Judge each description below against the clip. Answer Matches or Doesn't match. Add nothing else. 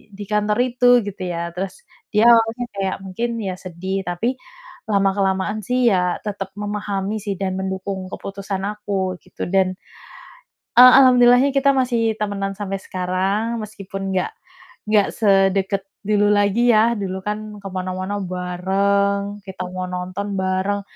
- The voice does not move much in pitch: Matches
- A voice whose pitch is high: Matches